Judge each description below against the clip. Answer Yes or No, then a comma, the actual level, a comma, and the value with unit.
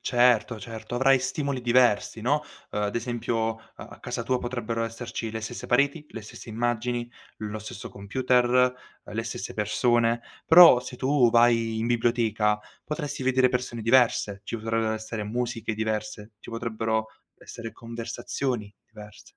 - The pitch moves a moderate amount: No, narrow, 2.0 semitones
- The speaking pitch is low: Yes, low, 115 Hz